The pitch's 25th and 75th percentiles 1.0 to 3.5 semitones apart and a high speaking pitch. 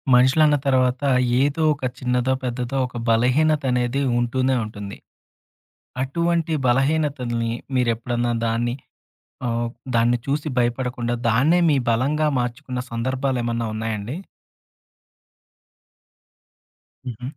No: narrow, 2.5 semitones; low, 125 Hz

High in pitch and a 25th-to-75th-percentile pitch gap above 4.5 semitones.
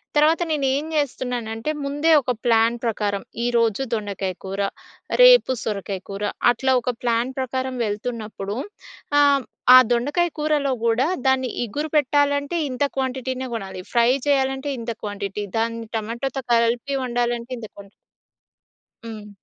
No: high, 245 Hz; average, 3.6 semitones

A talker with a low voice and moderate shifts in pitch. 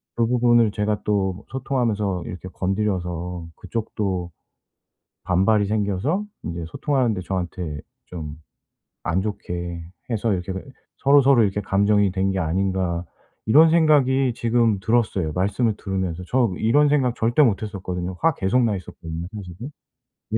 Yes: low, 100 Hz; average, 4.4 semitones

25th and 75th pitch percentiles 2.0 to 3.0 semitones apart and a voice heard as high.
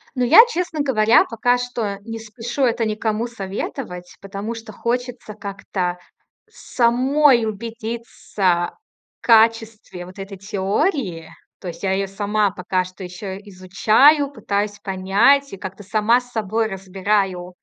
No: average, 3.5 semitones; high, 215 Hz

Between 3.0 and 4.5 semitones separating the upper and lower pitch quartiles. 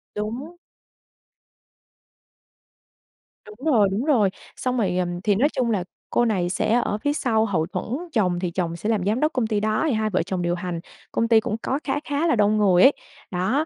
No: average, 5.0 semitones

